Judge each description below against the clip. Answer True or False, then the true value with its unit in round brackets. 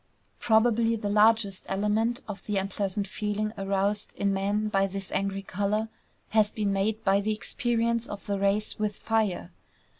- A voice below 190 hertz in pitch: False (205 Hz)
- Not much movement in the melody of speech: True (1.8 semitones)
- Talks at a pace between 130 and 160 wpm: True (155 wpm)